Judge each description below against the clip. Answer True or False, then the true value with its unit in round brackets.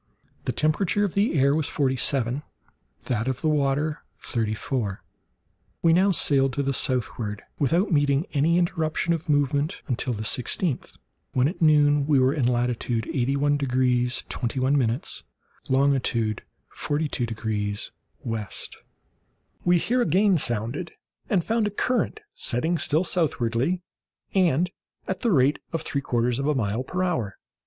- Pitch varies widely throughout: False (4.9 semitones)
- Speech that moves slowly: False (145 wpm)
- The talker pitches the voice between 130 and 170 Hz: True (140 Hz)